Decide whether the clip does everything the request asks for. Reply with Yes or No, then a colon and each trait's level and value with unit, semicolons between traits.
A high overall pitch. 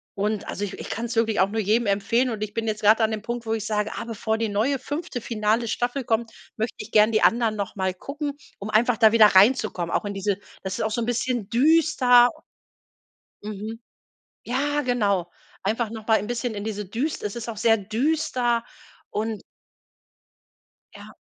Yes: high, 225 Hz